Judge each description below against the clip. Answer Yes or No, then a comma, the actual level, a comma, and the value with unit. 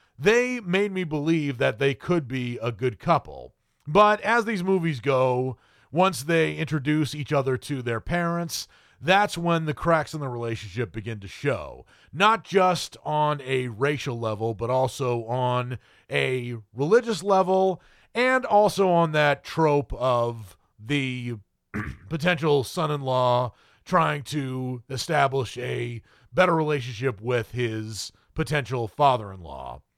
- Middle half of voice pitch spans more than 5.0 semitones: Yes, wide, 5.4 semitones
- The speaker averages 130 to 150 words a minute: Yes, average, 140 wpm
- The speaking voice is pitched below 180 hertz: Yes, medium, 140 Hz